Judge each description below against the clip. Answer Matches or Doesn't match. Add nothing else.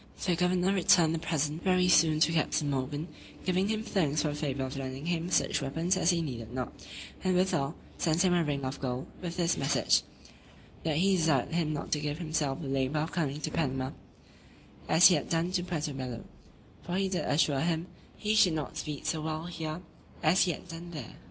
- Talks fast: Matches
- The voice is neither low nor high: Matches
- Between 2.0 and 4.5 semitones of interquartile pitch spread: Matches